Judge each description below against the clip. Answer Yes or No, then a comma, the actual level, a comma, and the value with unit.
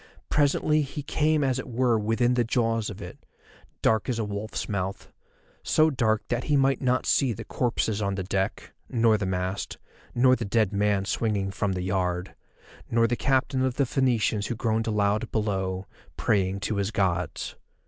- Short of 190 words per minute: Yes, average, 180 wpm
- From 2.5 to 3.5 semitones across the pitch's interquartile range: No, average, 4.0 semitones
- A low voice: Yes, low, 110 Hz